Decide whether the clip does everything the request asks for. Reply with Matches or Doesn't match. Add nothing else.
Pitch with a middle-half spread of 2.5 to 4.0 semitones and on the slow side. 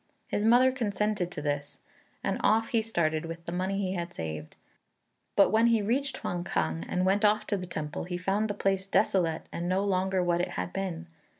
Doesn't match